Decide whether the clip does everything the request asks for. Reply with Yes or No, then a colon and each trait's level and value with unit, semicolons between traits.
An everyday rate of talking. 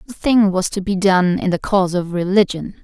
No: fast, 235 wpm